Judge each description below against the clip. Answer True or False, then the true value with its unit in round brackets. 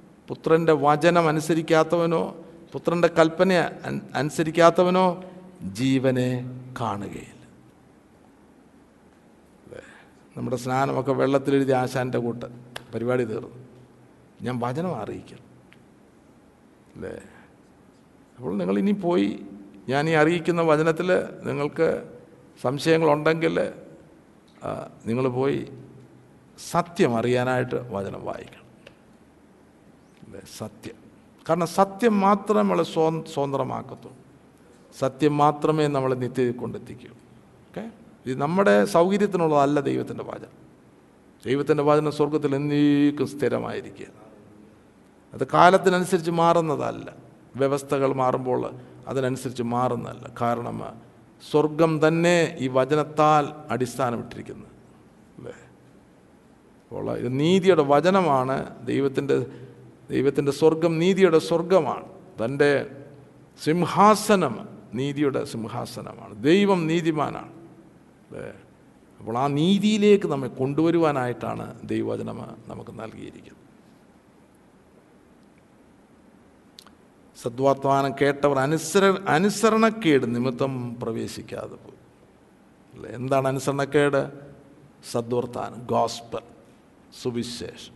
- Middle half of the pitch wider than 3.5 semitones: True (4.8 semitones)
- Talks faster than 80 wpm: False (75 wpm)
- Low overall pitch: False (145 Hz)